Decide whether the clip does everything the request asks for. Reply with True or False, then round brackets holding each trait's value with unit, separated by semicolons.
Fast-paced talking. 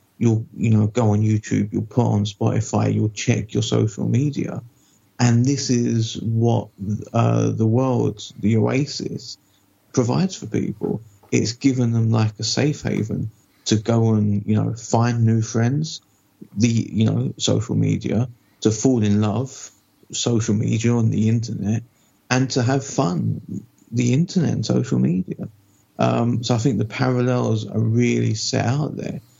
False (155 wpm)